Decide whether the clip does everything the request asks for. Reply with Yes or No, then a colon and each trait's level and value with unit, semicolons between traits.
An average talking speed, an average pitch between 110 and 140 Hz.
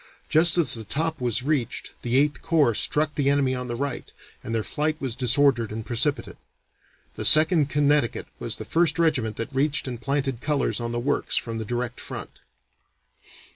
Yes: average, 180 wpm; low, 135 Hz